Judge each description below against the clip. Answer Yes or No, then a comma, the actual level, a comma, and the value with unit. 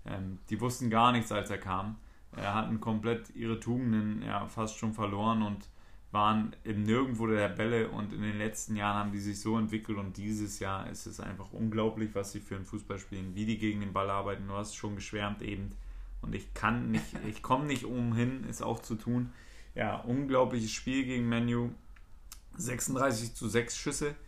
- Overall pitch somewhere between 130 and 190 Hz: No, low, 110 Hz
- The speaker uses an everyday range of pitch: No, narrow, 2.3 semitones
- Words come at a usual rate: No, fast, 195 wpm